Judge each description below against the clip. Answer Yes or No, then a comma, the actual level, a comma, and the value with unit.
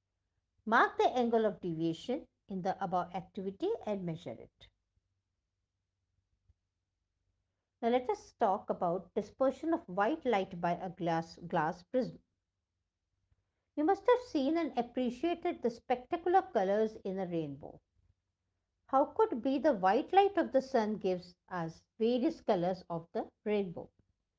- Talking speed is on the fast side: No, slow, 135 wpm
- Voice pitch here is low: No, high, 190 Hz